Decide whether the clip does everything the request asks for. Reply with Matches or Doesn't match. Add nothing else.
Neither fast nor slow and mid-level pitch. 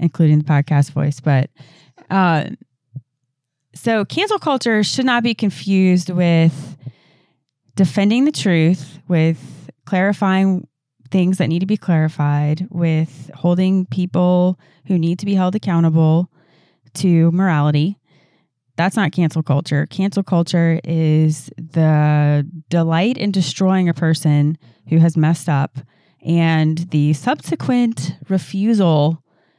Doesn't match